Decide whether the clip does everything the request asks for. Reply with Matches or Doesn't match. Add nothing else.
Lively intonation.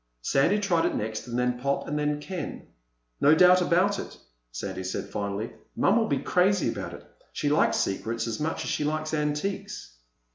Matches